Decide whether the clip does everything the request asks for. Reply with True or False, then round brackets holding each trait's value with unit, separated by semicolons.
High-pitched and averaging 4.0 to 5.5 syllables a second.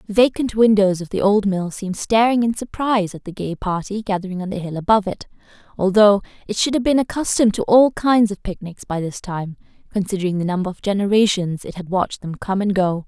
False (200 Hz; 6.0 syllables/s)